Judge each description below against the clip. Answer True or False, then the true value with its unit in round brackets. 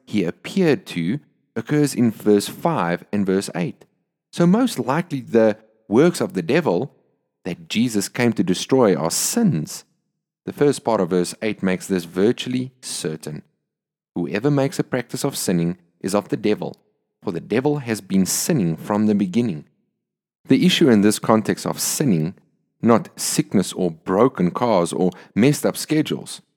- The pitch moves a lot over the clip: True (7.0 semitones)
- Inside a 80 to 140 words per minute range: False (160 wpm)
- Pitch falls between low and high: False (115 Hz)